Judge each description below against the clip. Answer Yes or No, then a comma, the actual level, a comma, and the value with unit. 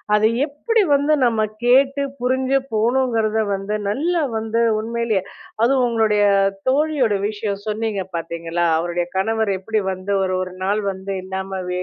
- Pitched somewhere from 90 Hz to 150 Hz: No, high, 220 Hz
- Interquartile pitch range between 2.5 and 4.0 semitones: No, average, 4.7 semitones